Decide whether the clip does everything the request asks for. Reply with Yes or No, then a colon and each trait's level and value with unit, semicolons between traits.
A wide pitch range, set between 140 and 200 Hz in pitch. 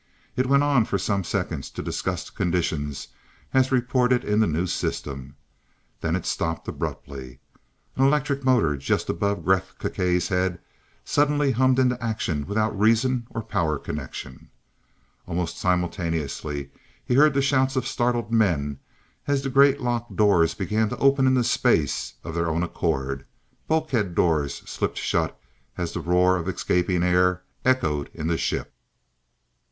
No: wide, 7.5 semitones; low, 100 Hz